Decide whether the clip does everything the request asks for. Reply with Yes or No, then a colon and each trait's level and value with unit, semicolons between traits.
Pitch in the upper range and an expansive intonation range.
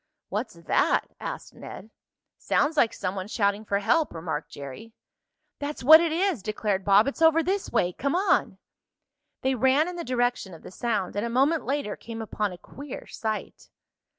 Yes: high, 235 Hz; wide, 6.7 semitones